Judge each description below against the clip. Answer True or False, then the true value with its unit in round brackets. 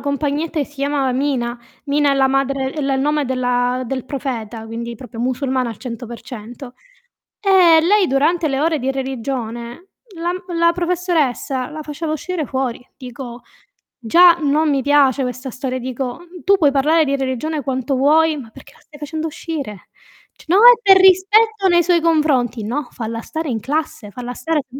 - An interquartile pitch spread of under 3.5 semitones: False (4.2 semitones)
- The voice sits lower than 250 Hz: False (275 Hz)